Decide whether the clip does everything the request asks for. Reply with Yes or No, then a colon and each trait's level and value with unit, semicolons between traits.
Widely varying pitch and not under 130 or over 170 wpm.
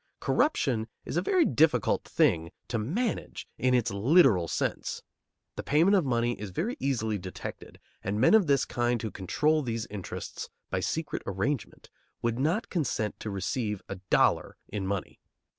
Yes: wide, 7.0 semitones; average, 160 wpm